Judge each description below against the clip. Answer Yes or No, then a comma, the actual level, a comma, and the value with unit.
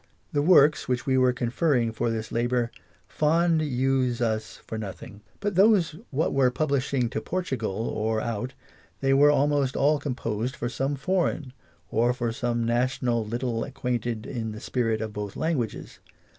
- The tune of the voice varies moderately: Yes, average, 3.7 semitones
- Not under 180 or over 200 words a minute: No, average, 155 wpm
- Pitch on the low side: Yes, low, 125 Hz